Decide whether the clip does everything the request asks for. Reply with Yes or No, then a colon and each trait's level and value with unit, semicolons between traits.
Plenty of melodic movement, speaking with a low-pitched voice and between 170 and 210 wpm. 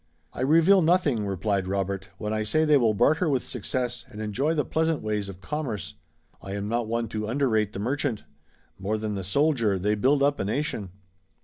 Yes: wide, 5.8 semitones; low, 110 Hz; average, 195 wpm